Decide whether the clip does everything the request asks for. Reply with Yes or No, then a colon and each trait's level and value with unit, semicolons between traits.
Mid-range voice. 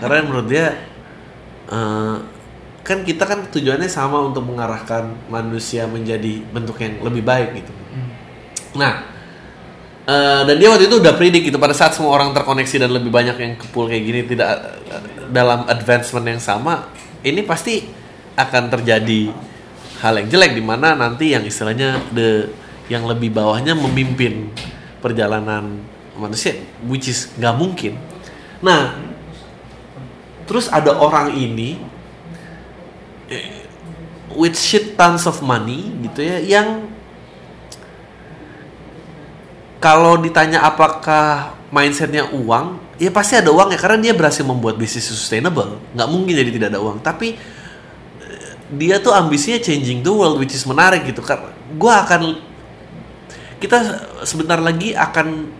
No: low, 130 Hz